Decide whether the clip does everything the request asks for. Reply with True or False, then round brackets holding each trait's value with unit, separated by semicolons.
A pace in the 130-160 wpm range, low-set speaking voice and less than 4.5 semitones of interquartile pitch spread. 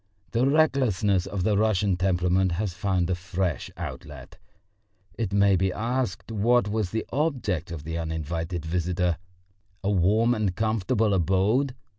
True (140 wpm; 95 Hz; 3.9 semitones)